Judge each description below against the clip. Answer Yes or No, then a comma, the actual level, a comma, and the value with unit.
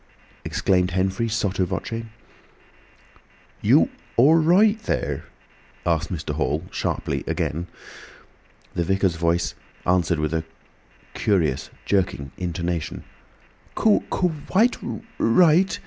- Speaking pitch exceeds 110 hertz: No, very low, 95 Hz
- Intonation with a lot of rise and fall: Yes, wide, 7.9 semitones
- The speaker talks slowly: Yes, slow, 85 wpm